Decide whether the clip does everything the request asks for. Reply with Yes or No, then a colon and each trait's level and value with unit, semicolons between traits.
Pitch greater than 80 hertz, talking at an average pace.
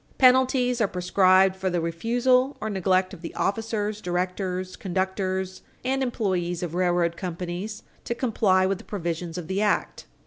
Yes: high, 190 Hz; average, 150 wpm